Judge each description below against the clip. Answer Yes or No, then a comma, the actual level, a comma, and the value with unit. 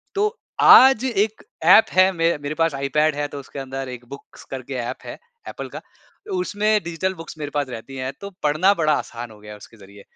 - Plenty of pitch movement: Yes, wide, 6.3 semitones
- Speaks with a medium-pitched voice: Yes, medium, 150 Hz